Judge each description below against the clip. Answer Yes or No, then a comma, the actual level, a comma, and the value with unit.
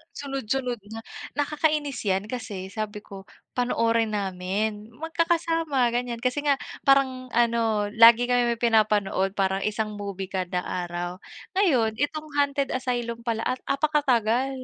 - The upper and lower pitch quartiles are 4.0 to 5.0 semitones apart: Yes, average, 4.6 semitones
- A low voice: No, high, 235 Hz